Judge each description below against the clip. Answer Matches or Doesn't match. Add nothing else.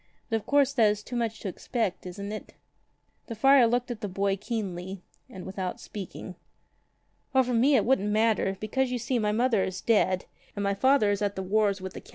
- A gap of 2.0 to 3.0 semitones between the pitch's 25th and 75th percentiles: Doesn't match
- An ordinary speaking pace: Doesn't match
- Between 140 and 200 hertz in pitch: Doesn't match